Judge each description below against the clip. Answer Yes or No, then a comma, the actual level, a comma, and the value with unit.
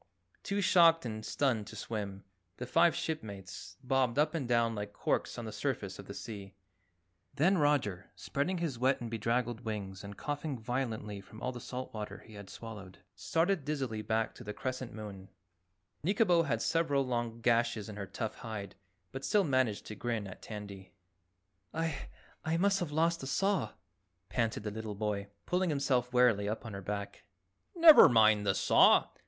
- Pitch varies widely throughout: Yes, wide, 5.7 semitones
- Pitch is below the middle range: Yes, low, 120 Hz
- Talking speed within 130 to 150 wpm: No, average, 175 wpm